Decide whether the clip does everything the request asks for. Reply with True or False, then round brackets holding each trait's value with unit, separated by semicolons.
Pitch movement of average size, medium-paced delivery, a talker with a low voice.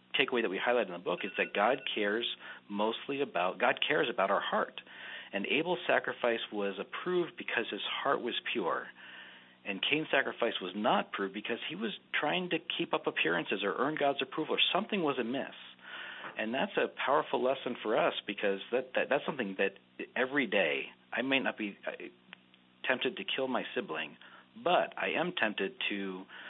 False (6.1 semitones; 180 wpm; 115 Hz)